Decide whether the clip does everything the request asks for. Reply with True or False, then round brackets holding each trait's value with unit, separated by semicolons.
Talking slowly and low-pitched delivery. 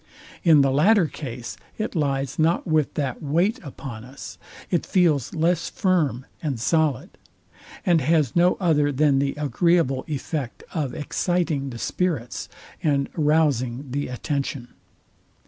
False (130 wpm; 150 Hz)